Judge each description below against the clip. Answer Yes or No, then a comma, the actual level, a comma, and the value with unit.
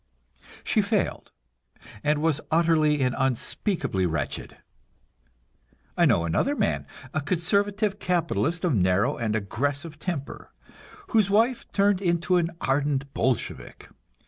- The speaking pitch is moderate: Yes, medium, 155 Hz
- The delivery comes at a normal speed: No, slow, 115 wpm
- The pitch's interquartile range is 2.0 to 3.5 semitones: No, wide, 5.6 semitones